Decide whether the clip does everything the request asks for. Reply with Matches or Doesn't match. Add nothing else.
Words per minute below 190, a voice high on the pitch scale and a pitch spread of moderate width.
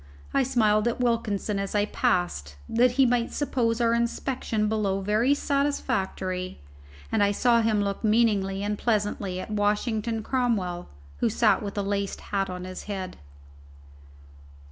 Matches